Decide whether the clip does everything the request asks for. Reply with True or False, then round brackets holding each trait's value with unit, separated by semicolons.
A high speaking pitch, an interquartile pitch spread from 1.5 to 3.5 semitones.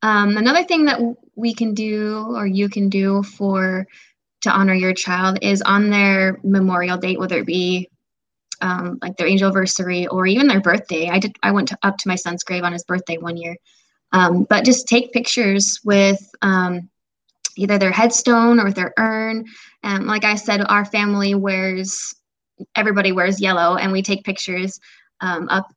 True (195 Hz; 2.5 semitones)